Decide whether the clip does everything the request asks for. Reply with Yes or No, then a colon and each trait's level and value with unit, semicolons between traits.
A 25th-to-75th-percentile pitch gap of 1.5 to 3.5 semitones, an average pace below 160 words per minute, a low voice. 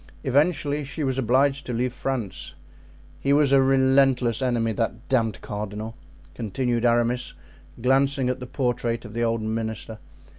Yes: average, 2.8 semitones; average, 145 wpm; low, 125 Hz